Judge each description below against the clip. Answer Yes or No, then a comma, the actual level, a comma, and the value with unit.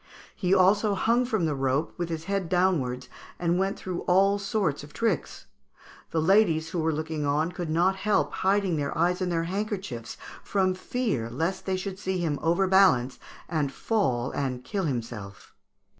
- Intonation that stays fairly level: No, average, 4.6 semitones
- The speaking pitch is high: No, medium, 175 Hz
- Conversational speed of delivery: Yes, average, 170 wpm